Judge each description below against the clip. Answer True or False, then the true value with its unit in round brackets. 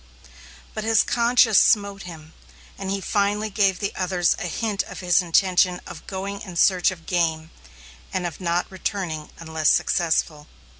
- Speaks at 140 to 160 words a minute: True (155 wpm)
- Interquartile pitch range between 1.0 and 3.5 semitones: True (2.9 semitones)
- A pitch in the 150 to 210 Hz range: True (185 Hz)